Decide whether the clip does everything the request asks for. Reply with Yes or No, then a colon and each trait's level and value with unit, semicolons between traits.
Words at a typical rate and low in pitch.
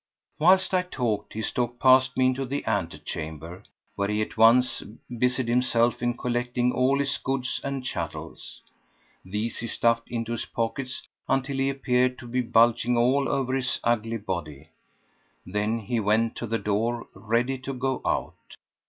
Yes: average, 160 wpm; low, 120 Hz